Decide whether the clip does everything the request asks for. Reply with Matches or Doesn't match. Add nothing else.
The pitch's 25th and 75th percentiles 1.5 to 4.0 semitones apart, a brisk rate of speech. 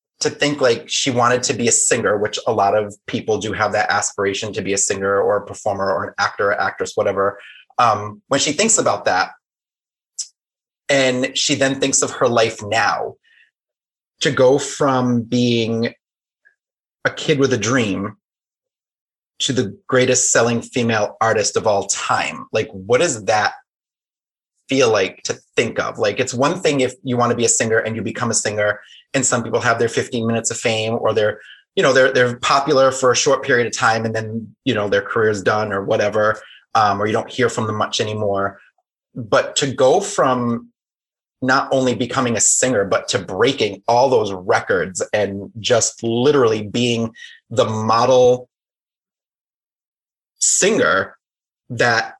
Doesn't match